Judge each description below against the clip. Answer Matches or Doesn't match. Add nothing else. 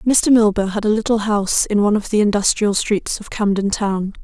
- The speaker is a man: Doesn't match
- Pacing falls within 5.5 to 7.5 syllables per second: Doesn't match